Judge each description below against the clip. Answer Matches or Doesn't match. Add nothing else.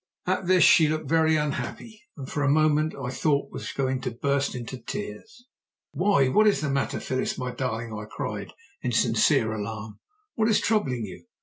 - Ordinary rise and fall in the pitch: Matches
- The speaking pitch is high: Doesn't match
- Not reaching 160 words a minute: Doesn't match